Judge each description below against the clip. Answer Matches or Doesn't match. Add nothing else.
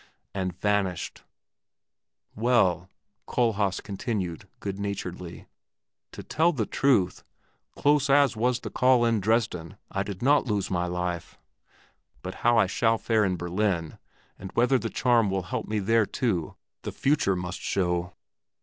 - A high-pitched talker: Doesn't match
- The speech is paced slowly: Doesn't match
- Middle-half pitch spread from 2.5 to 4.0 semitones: Doesn't match